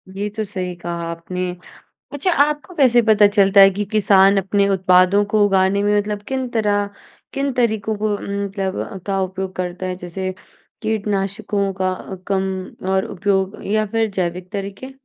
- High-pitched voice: Yes, high, 200 Hz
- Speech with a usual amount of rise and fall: No, narrow, 2.1 semitones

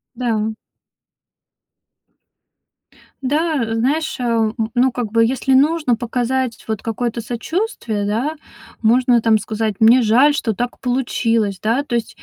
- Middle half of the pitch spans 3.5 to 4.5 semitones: No, average, 2.7 semitones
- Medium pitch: No, high, 235 Hz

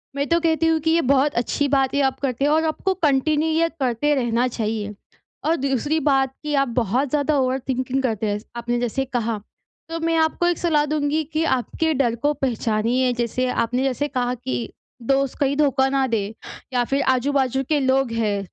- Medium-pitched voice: No, very high, 270 Hz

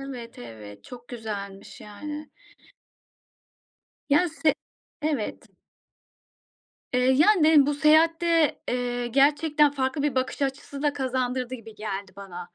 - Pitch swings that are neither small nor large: Yes, average, 4.9 semitones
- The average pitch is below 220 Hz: No, very high, 265 Hz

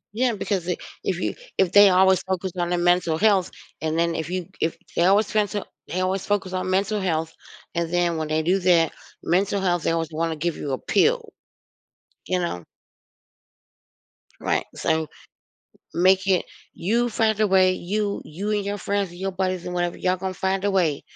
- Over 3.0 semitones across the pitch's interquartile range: No, narrow, 2.5 semitones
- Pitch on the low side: No, medium, 185 Hz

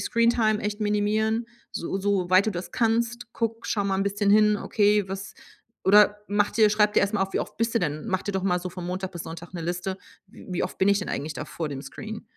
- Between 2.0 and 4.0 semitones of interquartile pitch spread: Yes, average, 2.7 semitones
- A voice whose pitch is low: No, high, 200 Hz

